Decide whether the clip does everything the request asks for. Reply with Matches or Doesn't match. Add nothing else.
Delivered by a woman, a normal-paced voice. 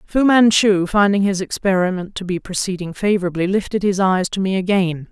Matches